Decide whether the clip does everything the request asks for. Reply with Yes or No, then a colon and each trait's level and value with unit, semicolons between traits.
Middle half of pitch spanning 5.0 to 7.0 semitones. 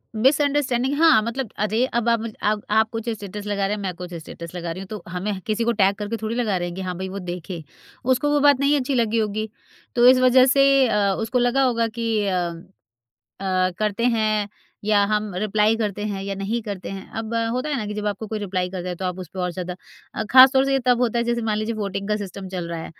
No: average, 3.6 semitones